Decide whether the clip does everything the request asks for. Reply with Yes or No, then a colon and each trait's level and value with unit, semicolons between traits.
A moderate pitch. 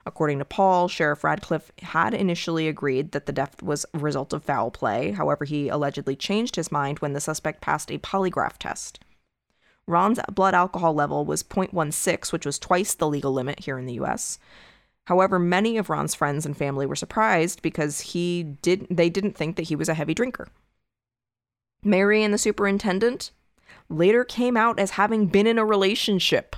Yes: medium, 165 Hz